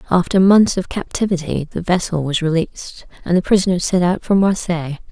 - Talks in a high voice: No, medium, 175 Hz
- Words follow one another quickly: No, average, 175 wpm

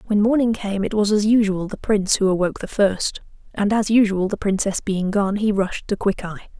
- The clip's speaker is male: No, female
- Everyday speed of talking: No, fast, 220 wpm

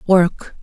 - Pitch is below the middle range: No, medium, 180 Hz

